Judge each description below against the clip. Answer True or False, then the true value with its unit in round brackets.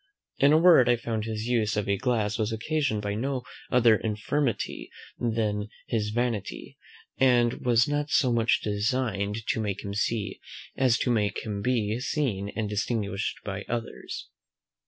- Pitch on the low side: True (110 Hz)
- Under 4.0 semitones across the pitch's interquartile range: True (3.1 semitones)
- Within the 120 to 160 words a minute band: True (155 wpm)